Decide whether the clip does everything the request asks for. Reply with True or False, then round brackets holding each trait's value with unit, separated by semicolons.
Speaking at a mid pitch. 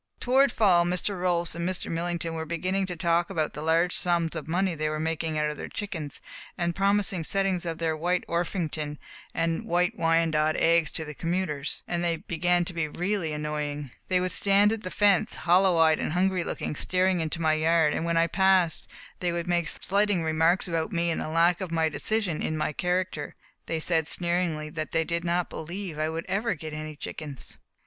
True (170 Hz)